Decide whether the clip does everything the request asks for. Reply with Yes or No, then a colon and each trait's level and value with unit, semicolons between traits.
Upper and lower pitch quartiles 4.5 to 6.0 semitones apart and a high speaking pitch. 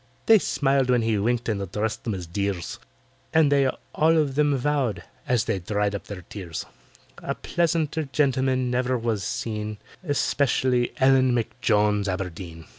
No: average, 5.0 semitones; low, 120 Hz